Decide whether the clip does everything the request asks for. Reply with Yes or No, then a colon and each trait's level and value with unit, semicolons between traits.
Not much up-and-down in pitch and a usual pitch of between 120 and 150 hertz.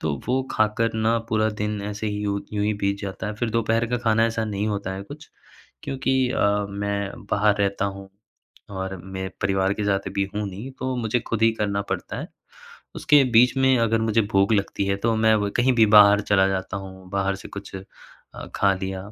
No: narrow, 2.3 semitones; low, 105 Hz